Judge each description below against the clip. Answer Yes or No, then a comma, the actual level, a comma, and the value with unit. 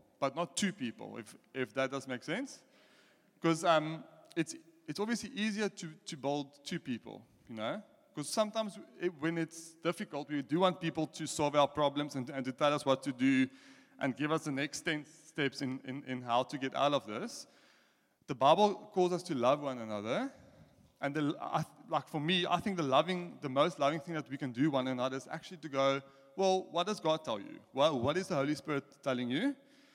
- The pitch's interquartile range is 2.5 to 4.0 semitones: No, average, 5.0 semitones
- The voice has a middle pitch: Yes, medium, 155 Hz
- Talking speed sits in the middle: No, fast, 215 wpm